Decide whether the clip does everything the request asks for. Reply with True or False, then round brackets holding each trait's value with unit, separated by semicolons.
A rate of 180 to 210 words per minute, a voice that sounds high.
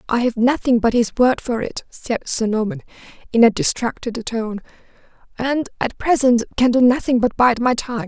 True (185 wpm; 240 Hz)